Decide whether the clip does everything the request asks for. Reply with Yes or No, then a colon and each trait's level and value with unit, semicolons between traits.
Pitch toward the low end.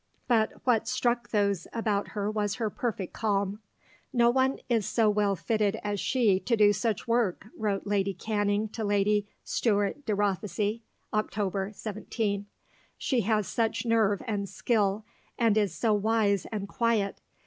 No: high, 210 Hz